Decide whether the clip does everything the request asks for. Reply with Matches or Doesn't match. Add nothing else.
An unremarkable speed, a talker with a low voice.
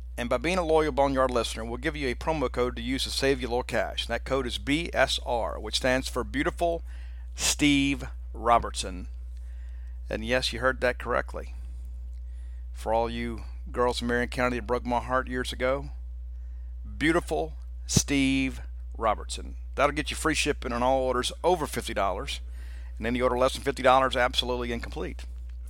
Matches